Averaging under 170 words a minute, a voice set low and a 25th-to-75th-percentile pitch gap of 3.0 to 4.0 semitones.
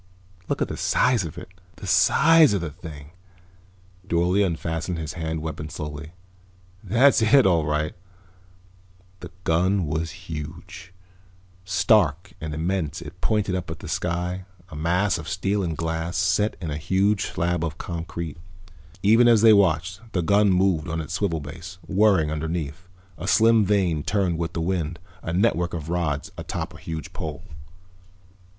Yes: average, 155 wpm; very low, 85 Hz; average, 3.3 semitones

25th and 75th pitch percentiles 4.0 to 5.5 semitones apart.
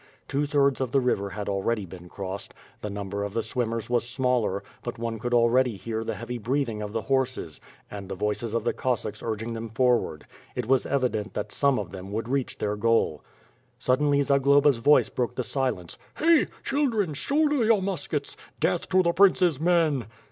Yes: average, 4.8 semitones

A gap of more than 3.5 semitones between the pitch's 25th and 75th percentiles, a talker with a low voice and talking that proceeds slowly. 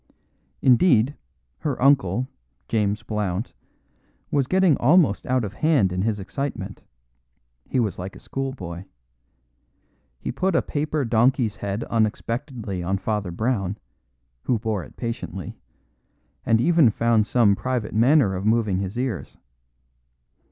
Yes: average, 4.7 semitones; low, 115 Hz; slow, 125 wpm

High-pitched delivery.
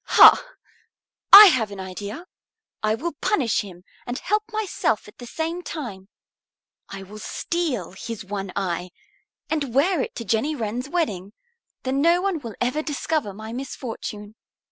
Yes: high, 240 Hz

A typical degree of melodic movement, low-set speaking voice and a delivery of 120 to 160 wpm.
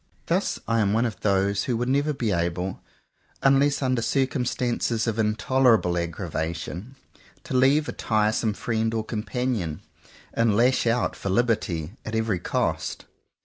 Yes: average, 4.0 semitones; low, 110 Hz; average, 145 wpm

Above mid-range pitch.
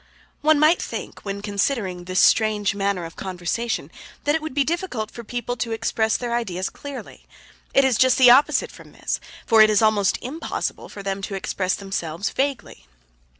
Yes: high, 220 Hz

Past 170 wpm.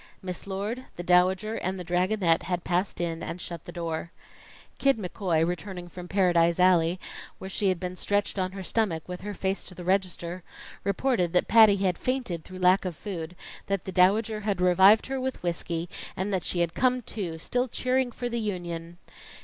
Yes: average, 190 wpm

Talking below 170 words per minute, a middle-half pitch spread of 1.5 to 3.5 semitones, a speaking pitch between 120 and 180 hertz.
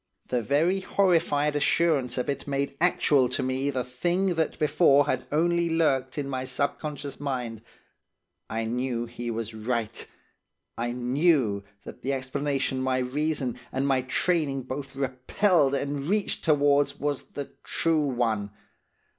Yes: average, 140 wpm; average, 3.0 semitones; medium, 140 Hz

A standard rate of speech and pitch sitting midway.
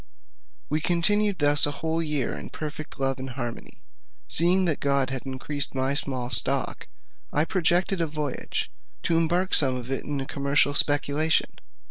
Yes: average, 160 wpm; medium, 145 Hz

